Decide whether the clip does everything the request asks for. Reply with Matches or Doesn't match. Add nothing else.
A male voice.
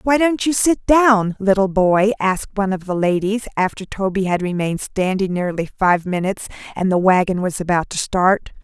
Doesn't match